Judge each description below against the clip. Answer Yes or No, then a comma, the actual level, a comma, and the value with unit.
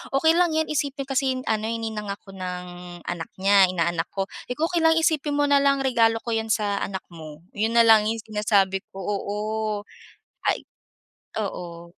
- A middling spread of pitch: No, wide, 5.9 semitones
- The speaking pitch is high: Yes, high, 220 Hz